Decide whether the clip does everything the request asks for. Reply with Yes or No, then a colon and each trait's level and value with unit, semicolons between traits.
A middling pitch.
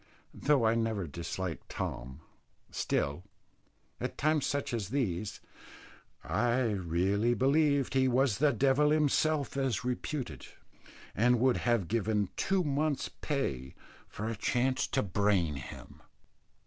No: low, 120 Hz